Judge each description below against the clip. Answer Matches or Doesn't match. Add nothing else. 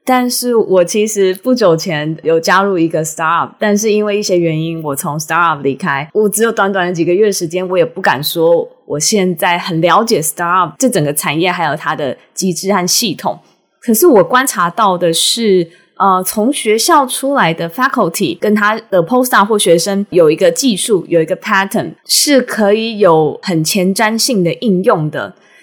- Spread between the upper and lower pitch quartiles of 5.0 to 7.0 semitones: Doesn't match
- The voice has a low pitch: Doesn't match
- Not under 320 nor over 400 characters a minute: Matches